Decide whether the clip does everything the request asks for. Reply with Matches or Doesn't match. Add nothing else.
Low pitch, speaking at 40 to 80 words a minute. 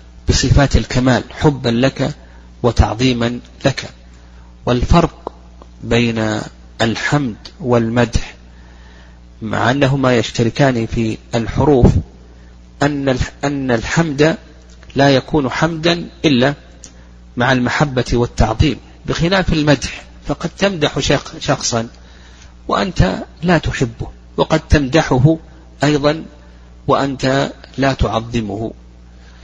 Matches